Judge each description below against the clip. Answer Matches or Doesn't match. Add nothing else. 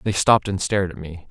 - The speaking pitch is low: Matches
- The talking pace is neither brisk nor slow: Doesn't match